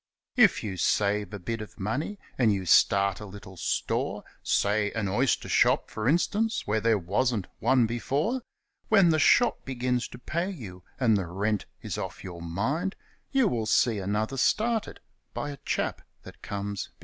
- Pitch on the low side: Yes, low, 110 Hz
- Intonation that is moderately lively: No, wide, 5.9 semitones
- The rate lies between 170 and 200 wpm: Yes, average, 175 wpm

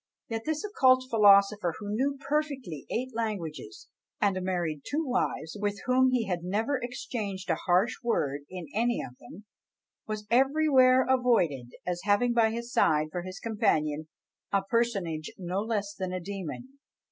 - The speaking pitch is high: Yes, high, 210 Hz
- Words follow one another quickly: No, average, 155 wpm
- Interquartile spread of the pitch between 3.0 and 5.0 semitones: No, wide, 5.6 semitones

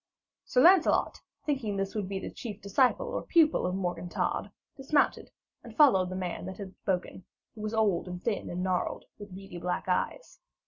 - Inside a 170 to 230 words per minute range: Yes, average, 185 wpm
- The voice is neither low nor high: No, high, 195 Hz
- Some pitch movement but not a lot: Yes, average, 4.7 semitones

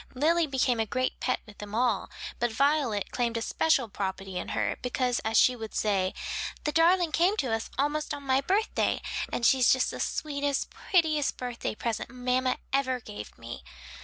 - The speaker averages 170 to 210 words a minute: Yes, average, 180 wpm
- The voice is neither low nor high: No, very high, 255 Hz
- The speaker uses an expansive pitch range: No, average, 4.5 semitones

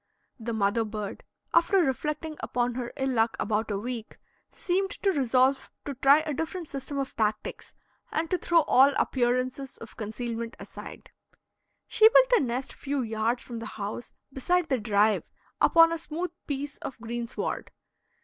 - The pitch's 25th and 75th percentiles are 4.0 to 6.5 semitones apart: Yes, average, 5.1 semitones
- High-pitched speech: Yes, very high, 255 Hz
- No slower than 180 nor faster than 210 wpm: No, average, 160 wpm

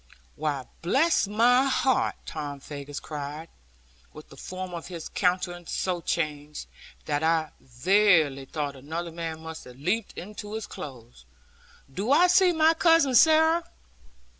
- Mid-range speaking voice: Yes, medium, 170 Hz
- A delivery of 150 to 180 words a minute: No, average, 140 wpm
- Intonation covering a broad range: Yes, wide, 7.1 semitones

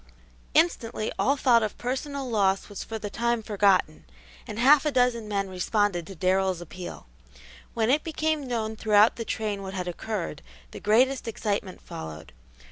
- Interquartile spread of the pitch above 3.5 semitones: Yes, average, 4.2 semitones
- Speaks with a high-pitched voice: Yes, high, 215 Hz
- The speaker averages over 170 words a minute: No, average, 160 wpm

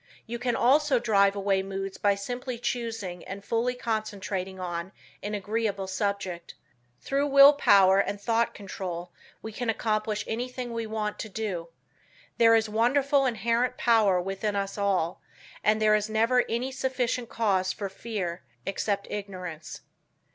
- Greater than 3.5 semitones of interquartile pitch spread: No, average, 3.2 semitones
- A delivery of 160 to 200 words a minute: No, average, 145 wpm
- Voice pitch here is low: No, high, 215 Hz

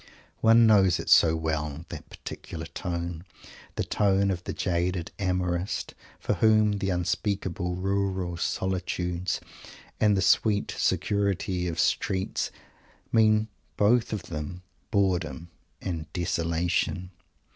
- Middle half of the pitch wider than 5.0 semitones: No, average, 2.7 semitones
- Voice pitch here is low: Yes, very low, 90 Hz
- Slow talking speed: Yes, slow, 115 wpm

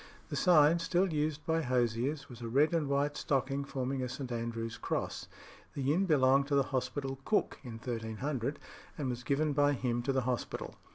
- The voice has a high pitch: No, low, 135 Hz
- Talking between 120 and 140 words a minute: No, average, 185 wpm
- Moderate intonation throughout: Yes, average, 3.1 semitones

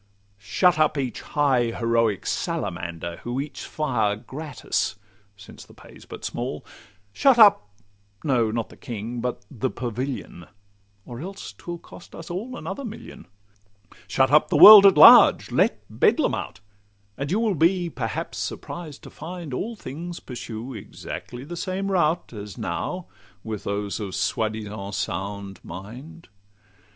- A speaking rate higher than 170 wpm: No, average, 145 wpm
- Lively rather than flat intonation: Yes, wide, 8.2 semitones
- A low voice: Yes, low, 125 Hz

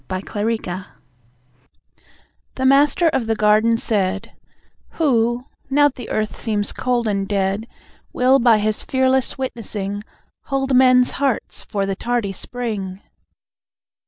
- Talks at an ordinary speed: No, slow, 120 wpm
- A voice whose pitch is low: No, high, 230 Hz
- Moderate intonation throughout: Yes, average, 4.1 semitones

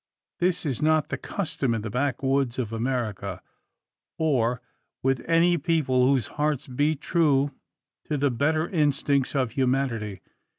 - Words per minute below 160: Yes, slow, 135 wpm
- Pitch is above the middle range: No, low, 135 Hz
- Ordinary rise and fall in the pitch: Yes, average, 3.6 semitones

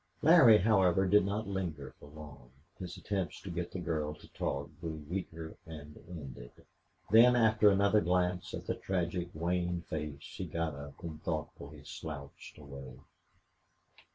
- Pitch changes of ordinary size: Yes, average, 4.2 semitones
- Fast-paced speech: No, average, 150 wpm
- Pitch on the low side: Yes, very low, 85 Hz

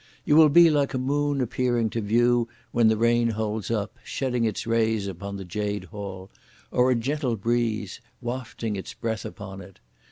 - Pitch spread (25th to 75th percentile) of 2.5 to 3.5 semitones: Yes, average, 3.1 semitones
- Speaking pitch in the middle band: No, low, 115 Hz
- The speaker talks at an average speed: Yes, average, 180 wpm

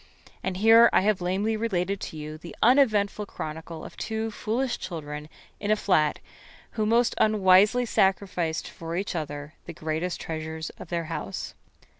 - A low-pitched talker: No, medium, 185 Hz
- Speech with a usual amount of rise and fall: Yes, average, 5.0 semitones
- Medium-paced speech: Yes, average, 155 wpm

